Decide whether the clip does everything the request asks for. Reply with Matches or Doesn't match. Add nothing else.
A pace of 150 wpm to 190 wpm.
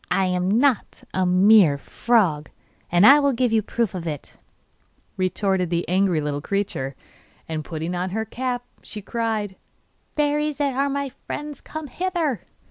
Matches